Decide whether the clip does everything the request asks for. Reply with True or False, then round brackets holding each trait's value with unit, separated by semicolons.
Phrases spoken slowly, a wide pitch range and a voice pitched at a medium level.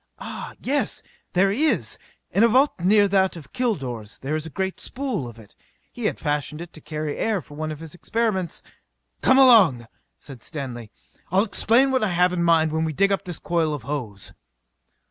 False (200 wpm; 6.2 semitones; 170 Hz)